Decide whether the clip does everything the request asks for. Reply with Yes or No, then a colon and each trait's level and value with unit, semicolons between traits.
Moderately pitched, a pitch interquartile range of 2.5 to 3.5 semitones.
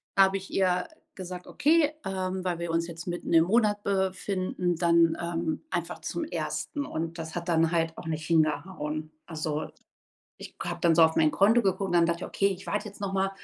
Yes: medium, 175 Hz; average, 2.8 semitones